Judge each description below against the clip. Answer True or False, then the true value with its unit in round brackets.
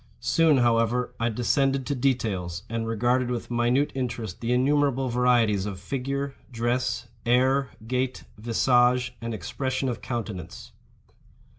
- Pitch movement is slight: True (2.2 semitones)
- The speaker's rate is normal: False (125 wpm)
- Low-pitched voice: True (125 Hz)